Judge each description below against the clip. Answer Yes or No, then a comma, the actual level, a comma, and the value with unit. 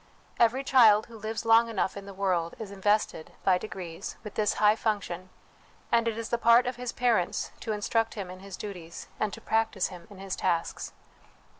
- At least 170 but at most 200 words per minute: Yes, average, 195 wpm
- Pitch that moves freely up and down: No, average, 3.1 semitones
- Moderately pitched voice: No, high, 210 Hz